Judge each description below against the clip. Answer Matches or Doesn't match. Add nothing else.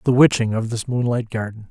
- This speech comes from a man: Matches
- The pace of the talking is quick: Matches